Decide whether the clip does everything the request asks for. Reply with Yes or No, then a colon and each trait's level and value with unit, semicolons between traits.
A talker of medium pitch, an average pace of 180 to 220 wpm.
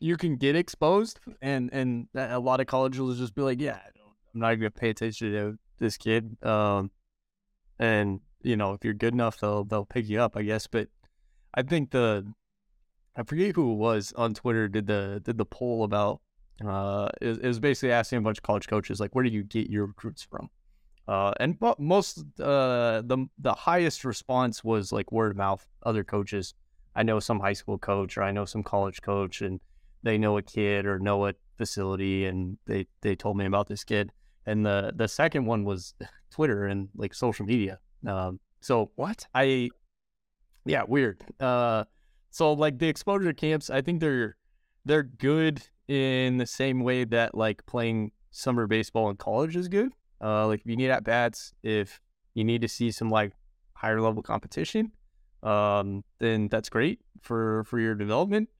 No: low, 110 Hz; average, 190 wpm